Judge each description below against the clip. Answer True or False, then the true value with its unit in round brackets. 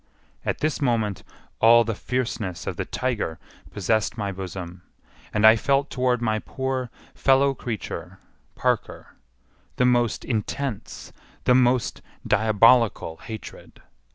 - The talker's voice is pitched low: True (115 Hz)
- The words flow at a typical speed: False (120 wpm)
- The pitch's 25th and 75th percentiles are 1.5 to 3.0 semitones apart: False (3.4 semitones)